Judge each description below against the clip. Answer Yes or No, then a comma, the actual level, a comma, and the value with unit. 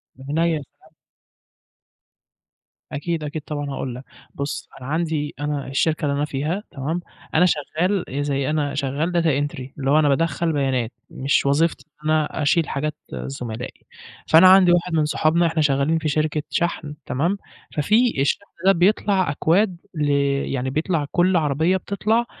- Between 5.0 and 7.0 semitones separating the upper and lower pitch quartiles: No, average, 3.3 semitones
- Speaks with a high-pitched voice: No, medium, 155 Hz